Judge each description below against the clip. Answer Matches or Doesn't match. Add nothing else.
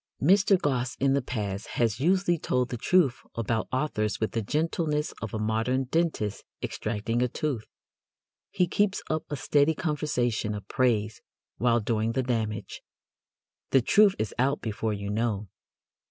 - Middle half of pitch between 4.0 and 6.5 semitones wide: Matches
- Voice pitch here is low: Matches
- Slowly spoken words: Doesn't match